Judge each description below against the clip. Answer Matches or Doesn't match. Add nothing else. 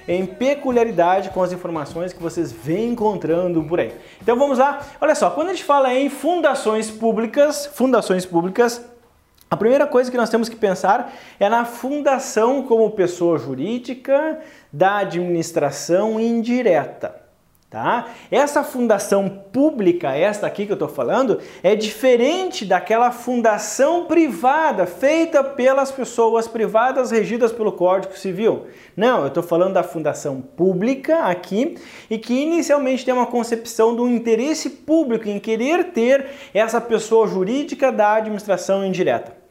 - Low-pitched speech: Doesn't match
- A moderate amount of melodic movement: Doesn't match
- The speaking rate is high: Doesn't match